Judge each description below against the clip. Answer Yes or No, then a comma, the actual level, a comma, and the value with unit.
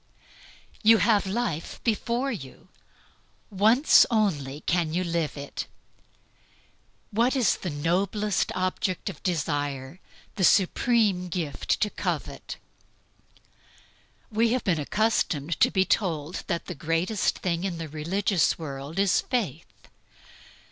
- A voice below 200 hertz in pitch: Yes, medium, 185 Hz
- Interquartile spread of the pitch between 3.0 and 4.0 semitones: No, average, 5.1 semitones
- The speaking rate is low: Yes, slow, 115 wpm